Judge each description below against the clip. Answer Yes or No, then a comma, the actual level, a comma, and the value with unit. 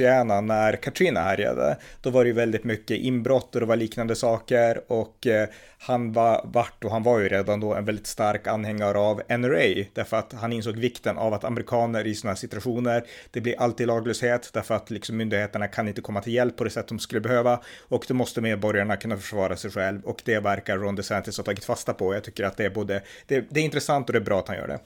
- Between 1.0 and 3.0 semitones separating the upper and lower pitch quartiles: Yes, narrow, 2.4 semitones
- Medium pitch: No, low, 115 Hz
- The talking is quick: Yes, fast, 235 wpm